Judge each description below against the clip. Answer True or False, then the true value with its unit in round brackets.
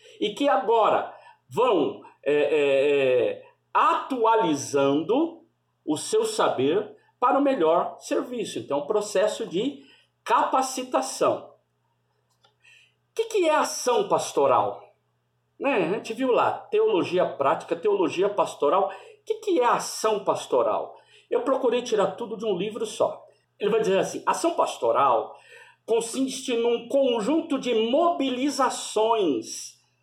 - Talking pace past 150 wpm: False (120 wpm)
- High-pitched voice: True (275 Hz)